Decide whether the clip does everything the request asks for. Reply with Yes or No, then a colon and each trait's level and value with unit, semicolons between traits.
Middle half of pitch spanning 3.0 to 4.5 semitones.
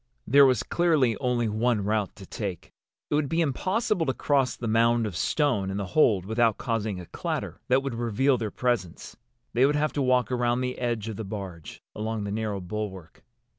Yes: average, 4.0 semitones